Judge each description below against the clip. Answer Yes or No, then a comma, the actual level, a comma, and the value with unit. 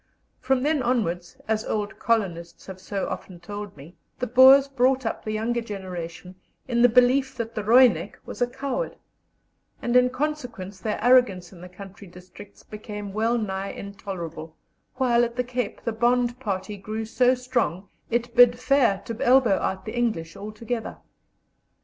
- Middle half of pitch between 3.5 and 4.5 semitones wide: Yes, average, 4.2 semitones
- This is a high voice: Yes, high, 225 Hz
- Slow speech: No, average, 160 wpm